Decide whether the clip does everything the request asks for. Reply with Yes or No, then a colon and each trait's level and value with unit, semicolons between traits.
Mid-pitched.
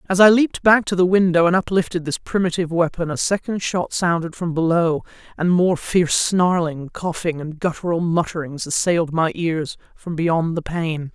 Yes: medium, 170 Hz